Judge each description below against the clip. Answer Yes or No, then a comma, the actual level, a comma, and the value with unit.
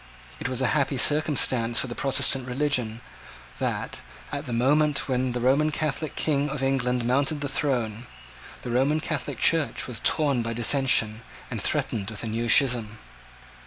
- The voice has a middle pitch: No, low, 130 Hz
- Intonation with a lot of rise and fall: No, average, 3.3 semitones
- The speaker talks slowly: No, average, 165 wpm